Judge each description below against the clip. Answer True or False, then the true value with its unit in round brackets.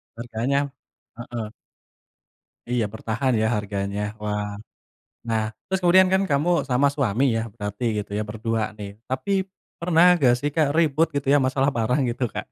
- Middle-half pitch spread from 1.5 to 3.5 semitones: False (4.5 semitones)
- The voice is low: True (125 Hz)